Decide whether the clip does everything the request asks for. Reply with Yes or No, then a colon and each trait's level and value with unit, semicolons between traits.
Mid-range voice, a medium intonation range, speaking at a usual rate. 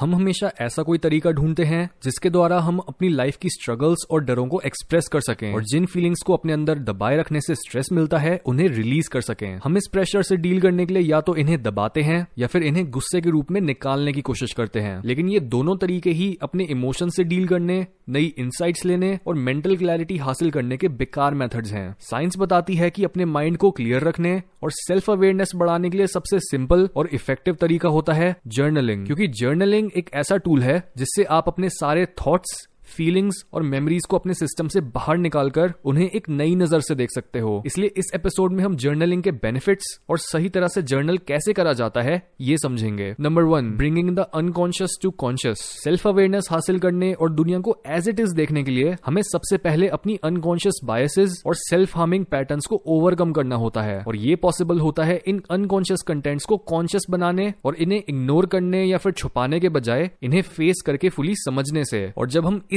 No: medium, 170 Hz; average, 4.6 semitones; fast, 205 wpm